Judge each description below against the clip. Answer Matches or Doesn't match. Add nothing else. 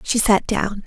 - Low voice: Doesn't match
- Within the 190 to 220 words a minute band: Matches